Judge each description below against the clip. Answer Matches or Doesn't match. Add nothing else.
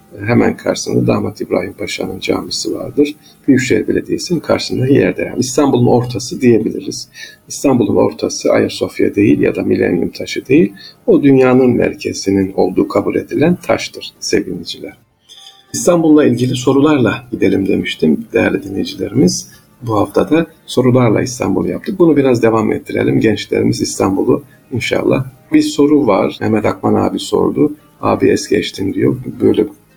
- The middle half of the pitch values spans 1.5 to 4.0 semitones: Doesn't match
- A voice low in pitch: Matches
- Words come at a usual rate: Matches